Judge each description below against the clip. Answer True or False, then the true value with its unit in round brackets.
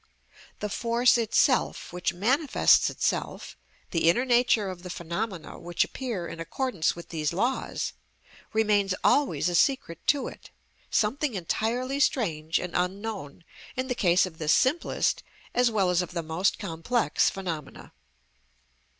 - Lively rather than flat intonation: True (6.1 semitones)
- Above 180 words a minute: False (140 wpm)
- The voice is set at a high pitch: True (195 Hz)